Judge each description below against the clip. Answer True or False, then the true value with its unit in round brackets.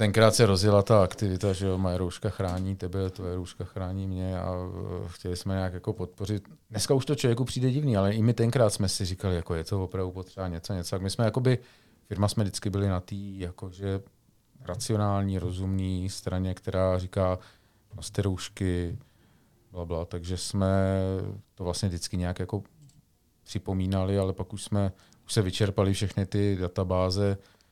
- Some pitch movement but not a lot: False (2.2 semitones)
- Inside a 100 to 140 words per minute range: False (170 wpm)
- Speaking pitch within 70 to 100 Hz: True (95 Hz)